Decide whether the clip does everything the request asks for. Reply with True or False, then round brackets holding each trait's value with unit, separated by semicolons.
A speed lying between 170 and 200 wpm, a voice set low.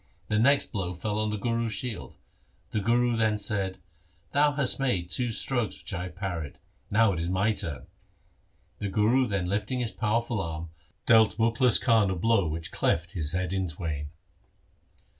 True (180 wpm; 105 Hz)